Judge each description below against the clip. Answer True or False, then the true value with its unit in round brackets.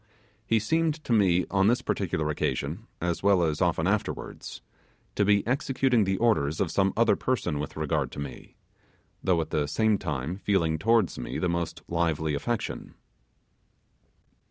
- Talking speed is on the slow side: False (155 wpm)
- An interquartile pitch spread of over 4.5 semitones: True (5.6 semitones)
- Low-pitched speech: True (95 Hz)